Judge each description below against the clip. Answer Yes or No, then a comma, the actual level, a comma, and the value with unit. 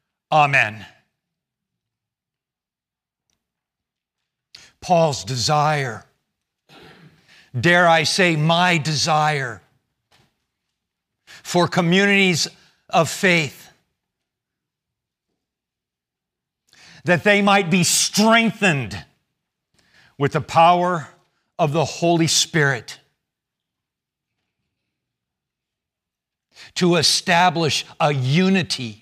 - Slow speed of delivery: Yes, slow, 60 wpm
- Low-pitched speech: No, medium, 165 Hz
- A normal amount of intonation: Yes, average, 4.5 semitones